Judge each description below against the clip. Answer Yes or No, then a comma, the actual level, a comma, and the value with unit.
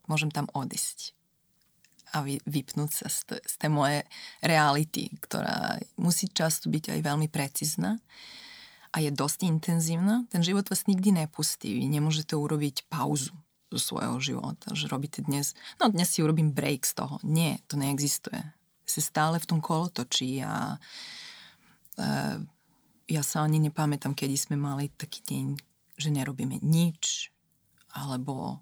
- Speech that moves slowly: No, average, 140 wpm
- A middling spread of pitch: Yes, average, 3.0 semitones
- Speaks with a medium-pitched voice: Yes, medium, 155 Hz